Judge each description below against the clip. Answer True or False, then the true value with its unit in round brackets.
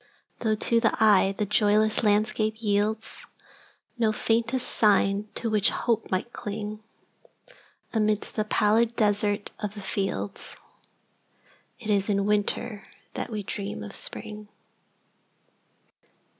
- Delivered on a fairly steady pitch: True (1.3 semitones)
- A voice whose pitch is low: False (210 Hz)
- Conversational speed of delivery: False (110 wpm)